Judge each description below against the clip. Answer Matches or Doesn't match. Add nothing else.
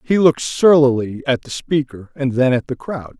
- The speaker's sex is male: Matches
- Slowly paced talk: Doesn't match